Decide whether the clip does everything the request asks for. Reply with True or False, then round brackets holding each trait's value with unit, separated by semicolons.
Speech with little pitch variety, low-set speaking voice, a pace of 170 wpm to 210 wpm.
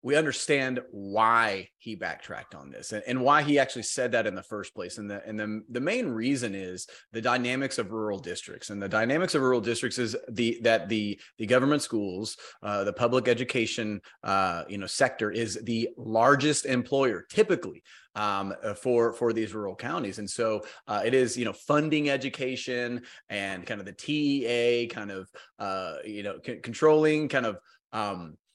False (3.5 semitones; 120 Hz; 185 wpm)